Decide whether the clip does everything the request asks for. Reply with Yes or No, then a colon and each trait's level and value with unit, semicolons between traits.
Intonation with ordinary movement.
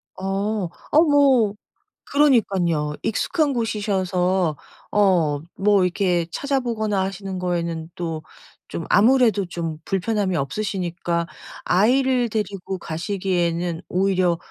Yes: average, 3.8 semitones